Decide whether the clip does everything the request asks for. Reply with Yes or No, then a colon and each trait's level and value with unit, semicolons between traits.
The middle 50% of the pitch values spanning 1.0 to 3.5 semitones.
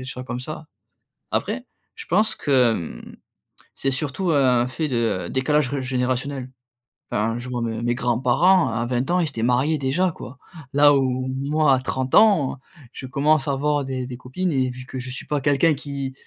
Yes: average, 2.8 semitones